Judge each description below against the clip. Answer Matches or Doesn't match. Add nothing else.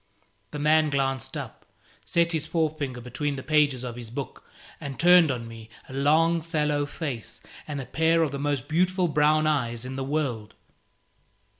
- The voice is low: Doesn't match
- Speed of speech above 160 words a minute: Matches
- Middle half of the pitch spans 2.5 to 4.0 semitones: Matches